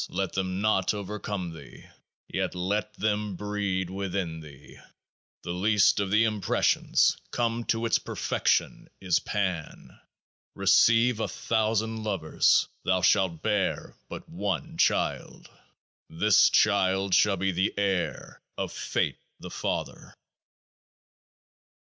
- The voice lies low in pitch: Yes, low, 100 Hz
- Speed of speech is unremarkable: No, slow, 120 wpm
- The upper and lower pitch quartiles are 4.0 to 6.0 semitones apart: No, narrow, 2.5 semitones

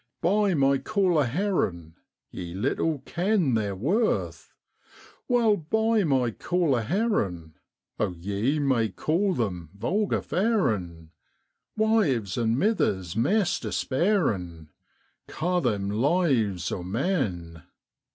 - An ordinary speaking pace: No, slow, 105 wpm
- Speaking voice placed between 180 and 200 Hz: No, low, 135 Hz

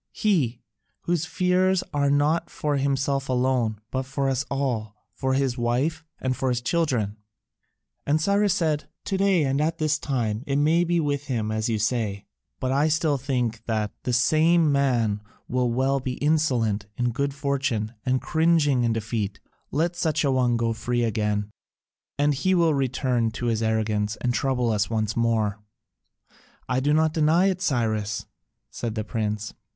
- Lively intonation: No, average, 4.8 semitones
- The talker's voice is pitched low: Yes, low, 130 Hz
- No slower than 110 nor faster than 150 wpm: No, average, 165 wpm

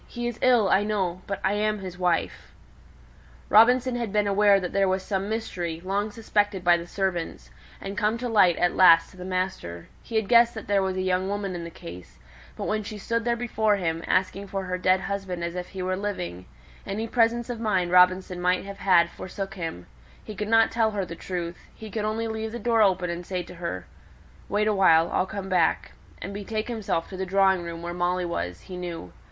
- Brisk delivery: Yes, fast, 220 wpm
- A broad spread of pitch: No, average, 3.1 semitones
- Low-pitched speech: No, high, 195 Hz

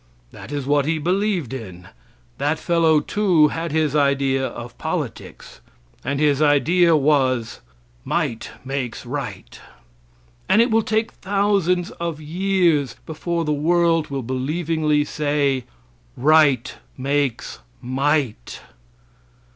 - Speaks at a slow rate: Yes, slow, 115 wpm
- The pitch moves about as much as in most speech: Yes, average, 3.8 semitones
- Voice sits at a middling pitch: Yes, medium, 150 Hz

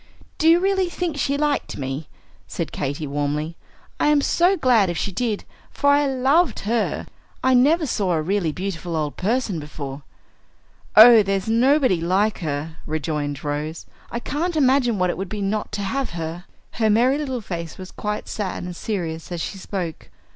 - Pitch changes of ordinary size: No, wide, 8.0 semitones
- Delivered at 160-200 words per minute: Yes, average, 175 wpm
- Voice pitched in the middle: No, high, 200 Hz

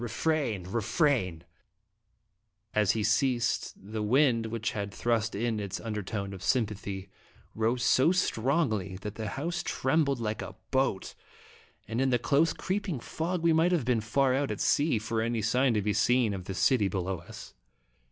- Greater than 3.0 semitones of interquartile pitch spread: Yes, average, 4.6 semitones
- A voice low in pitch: Yes, low, 115 Hz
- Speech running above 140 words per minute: Yes, average, 170 wpm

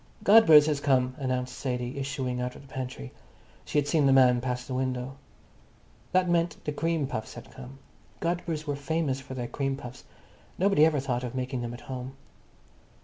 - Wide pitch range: No, average, 2.9 semitones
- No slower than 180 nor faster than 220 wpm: Yes, average, 185 wpm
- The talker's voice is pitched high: No, low, 135 Hz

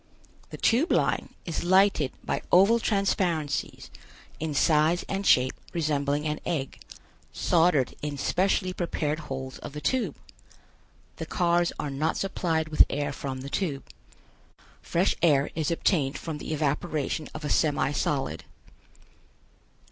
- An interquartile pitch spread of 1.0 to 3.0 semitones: No, average, 3.5 semitones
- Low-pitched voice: No, medium, 155 Hz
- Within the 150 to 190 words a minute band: No, slow, 135 wpm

